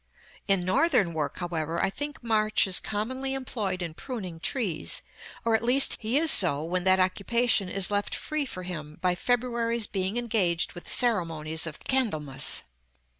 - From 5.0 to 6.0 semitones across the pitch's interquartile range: Yes, wide, 5.4 semitones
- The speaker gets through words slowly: No, average, 165 wpm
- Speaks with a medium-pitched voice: No, high, 195 Hz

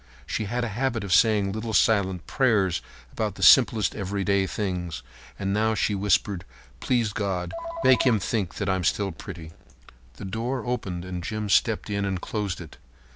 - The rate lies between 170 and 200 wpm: Yes, average, 175 wpm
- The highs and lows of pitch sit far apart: No, average, 2.9 semitones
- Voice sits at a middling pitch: No, low, 100 Hz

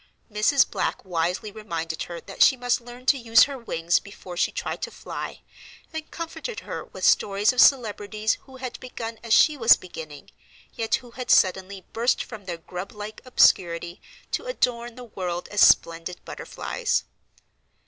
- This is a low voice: No, high, 215 Hz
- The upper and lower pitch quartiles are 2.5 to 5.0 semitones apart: No, wide, 5.4 semitones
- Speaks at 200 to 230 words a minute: No, average, 165 wpm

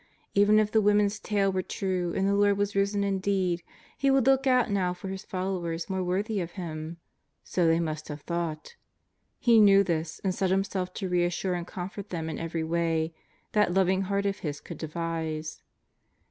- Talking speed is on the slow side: No, average, 190 wpm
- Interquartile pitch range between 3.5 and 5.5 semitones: No, average, 3.0 semitones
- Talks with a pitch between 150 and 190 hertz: Yes, medium, 185 Hz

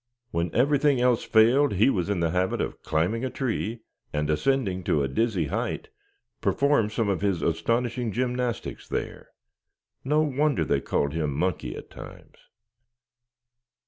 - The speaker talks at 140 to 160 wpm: Yes, average, 145 wpm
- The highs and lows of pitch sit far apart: Yes, wide, 6.8 semitones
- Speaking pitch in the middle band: No, low, 110 Hz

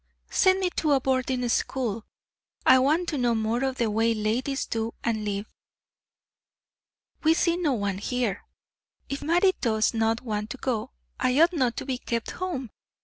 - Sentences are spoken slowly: No, average, 165 wpm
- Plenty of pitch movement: No, average, 3.9 semitones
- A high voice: Yes, very high, 250 Hz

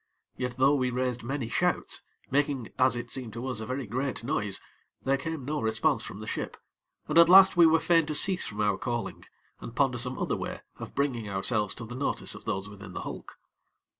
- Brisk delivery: Yes, fast, 215 wpm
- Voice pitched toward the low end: Yes, low, 125 Hz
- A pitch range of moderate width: Yes, average, 3.8 semitones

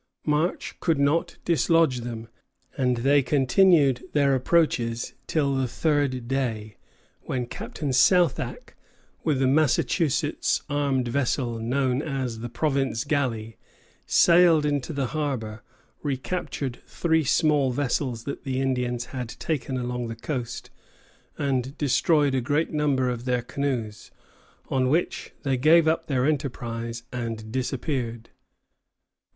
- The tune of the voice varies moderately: Yes, average, 3.3 semitones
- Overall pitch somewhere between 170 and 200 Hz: No, low, 135 Hz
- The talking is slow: Yes, slow, 125 wpm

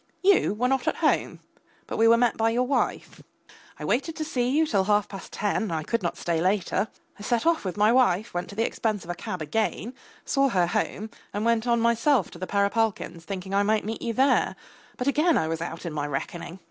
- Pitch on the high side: Yes, high, 215 Hz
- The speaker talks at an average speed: No, fast, 230 wpm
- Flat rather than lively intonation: No, average, 4.6 semitones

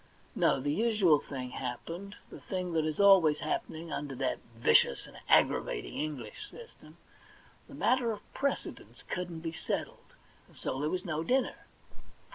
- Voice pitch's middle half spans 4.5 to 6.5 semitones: Yes, wide, 5.5 semitones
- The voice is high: No, medium, 165 Hz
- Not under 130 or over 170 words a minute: Yes, average, 160 wpm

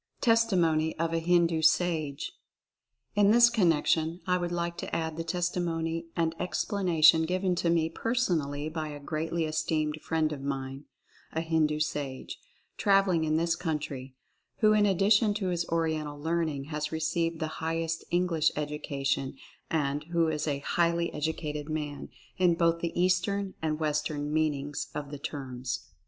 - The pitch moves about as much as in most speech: No, narrow, 2.3 semitones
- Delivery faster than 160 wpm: No, average, 155 wpm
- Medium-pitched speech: Yes, medium, 160 Hz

